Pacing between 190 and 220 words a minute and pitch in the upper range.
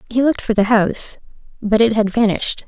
Yes: average, 200 wpm; high, 220 Hz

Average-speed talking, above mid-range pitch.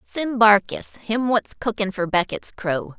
Yes: average, 160 wpm; high, 210 Hz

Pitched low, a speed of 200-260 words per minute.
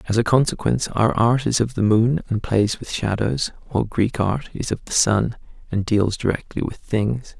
Yes: low, 110 Hz; fast, 205 wpm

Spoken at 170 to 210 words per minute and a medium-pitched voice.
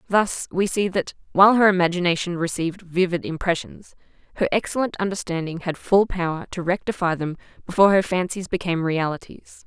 No: average, 150 wpm; medium, 180 Hz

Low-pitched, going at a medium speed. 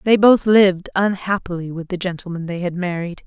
No: medium, 185 Hz; average, 185 wpm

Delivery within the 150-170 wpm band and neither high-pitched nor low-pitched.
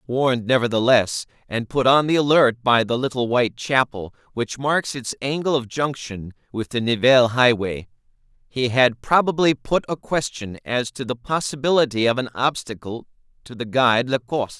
No: average, 160 wpm; low, 125 Hz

